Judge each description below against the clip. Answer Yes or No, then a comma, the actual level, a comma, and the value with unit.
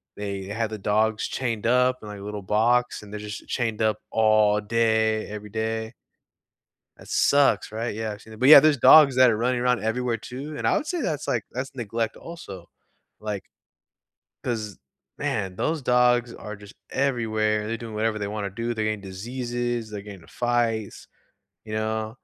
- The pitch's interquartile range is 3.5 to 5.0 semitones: No, narrow, 2.5 semitones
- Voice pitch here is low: Yes, low, 110 Hz